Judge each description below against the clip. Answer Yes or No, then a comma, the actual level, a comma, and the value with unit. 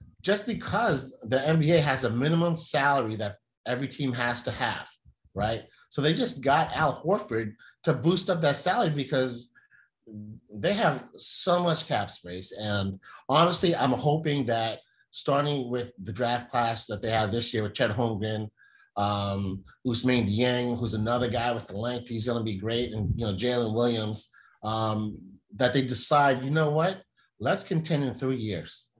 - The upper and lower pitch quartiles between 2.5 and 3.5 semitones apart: No, average, 4.5 semitones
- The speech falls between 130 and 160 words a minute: No, average, 170 wpm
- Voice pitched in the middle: No, low, 120 Hz